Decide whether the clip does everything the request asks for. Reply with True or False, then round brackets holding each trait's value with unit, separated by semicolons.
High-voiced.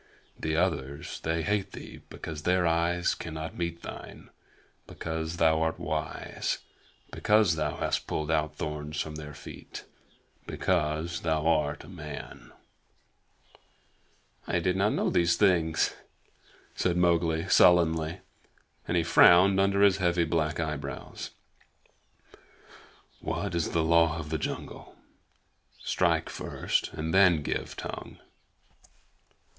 False (80 Hz)